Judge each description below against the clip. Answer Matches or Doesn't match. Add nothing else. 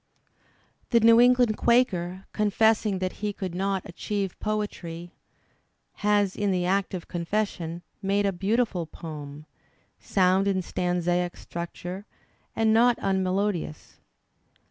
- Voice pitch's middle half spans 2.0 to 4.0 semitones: Matches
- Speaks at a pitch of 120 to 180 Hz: Doesn't match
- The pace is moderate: Doesn't match